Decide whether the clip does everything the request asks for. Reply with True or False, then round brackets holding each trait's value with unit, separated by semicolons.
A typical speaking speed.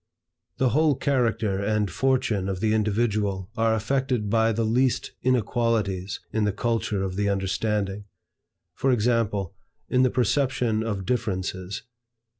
False (130 wpm)